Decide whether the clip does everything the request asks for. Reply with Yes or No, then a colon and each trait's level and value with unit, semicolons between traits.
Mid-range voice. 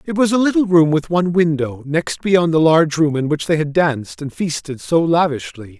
Yes: medium, 160 Hz